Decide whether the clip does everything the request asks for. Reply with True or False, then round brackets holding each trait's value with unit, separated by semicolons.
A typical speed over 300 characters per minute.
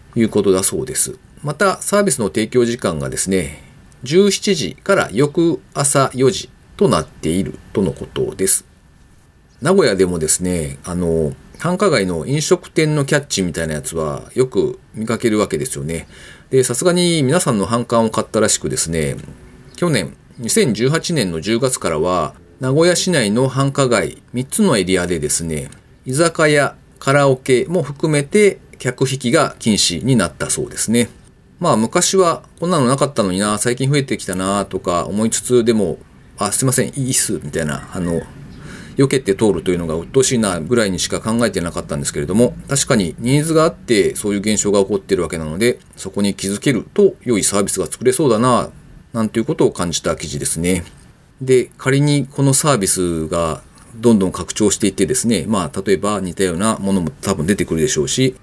True (365 characters per minute)